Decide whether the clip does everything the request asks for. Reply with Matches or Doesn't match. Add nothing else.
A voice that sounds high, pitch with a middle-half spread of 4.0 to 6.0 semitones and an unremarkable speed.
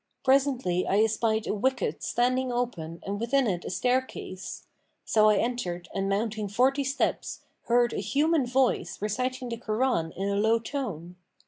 Matches